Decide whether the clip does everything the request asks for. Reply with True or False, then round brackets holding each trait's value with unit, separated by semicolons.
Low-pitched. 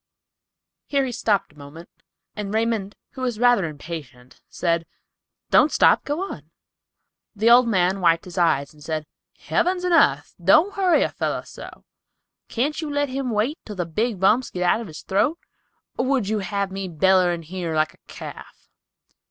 False (200 Hz)